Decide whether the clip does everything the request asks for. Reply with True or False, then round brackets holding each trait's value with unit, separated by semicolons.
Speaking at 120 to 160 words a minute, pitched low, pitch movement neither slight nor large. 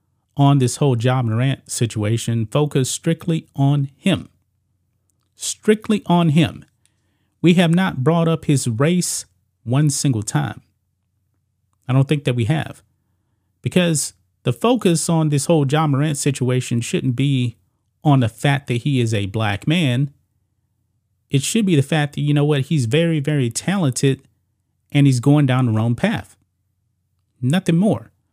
False (155 wpm; 130 Hz; 5.8 semitones)